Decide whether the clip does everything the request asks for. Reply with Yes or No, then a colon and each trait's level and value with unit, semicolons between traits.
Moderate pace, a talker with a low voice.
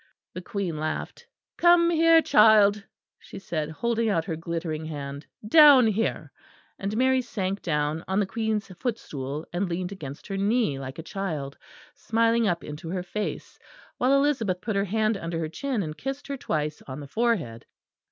No: average, 170 wpm; high, 195 Hz